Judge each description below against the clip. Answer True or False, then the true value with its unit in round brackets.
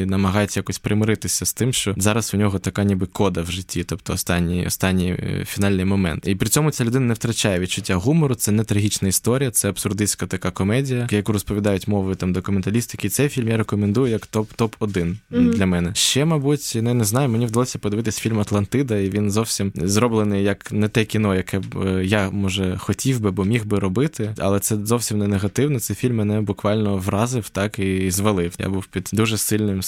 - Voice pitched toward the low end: True (105 Hz)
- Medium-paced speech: False (190 wpm)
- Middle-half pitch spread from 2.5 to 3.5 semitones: True (2.8 semitones)